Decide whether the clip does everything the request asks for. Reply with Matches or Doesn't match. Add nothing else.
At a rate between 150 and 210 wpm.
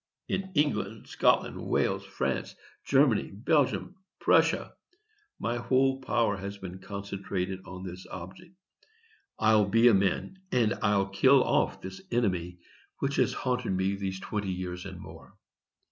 Doesn't match